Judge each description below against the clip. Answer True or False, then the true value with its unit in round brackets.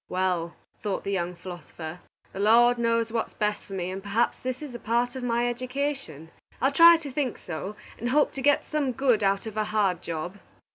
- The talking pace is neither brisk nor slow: False (210 wpm)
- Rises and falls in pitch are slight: False (5.2 semitones)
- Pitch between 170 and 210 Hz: False (225 Hz)